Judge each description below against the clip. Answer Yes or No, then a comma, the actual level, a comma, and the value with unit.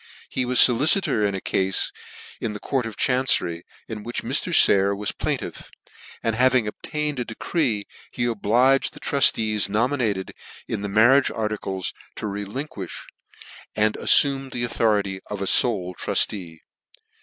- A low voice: Yes, low, 110 Hz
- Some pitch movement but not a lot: Yes, average, 4.1 semitones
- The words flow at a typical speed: Yes, average, 150 wpm